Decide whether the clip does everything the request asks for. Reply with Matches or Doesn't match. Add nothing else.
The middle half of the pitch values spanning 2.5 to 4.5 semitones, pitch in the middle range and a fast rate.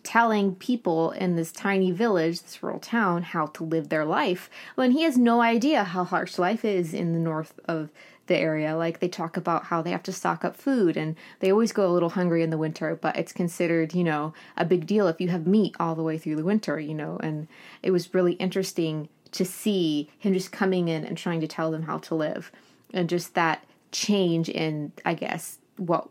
Matches